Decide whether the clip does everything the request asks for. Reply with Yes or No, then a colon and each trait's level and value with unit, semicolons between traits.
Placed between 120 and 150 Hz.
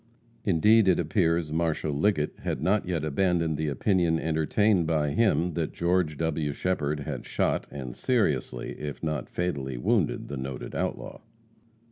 No: very low, 80 Hz